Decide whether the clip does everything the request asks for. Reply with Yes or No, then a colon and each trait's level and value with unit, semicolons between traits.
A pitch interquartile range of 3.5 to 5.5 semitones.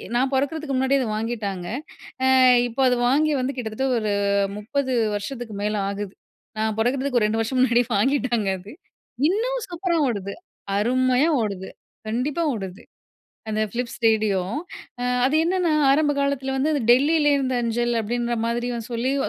Yes: average, 4.1 semitones